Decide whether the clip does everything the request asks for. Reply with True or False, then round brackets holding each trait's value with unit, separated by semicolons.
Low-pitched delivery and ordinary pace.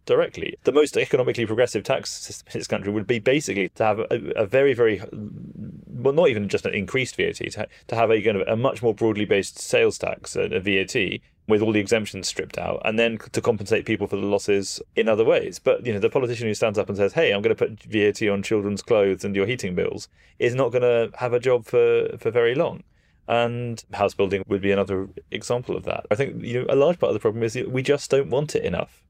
False (115 Hz; 235 wpm)